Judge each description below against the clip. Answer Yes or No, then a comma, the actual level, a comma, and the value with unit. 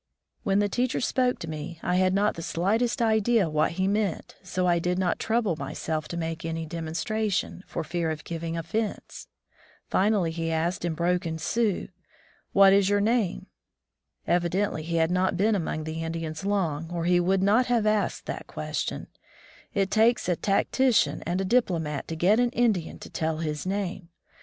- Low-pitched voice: No, medium, 180 Hz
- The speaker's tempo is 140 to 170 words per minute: No, average, 180 wpm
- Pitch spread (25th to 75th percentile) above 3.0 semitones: Yes, average, 4.0 semitones